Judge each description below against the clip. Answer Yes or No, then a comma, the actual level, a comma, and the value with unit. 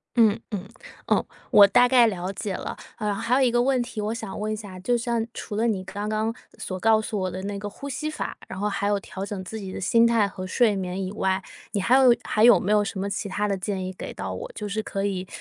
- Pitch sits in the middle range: No, high, 210 Hz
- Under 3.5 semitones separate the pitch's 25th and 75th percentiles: Yes, average, 3.0 semitones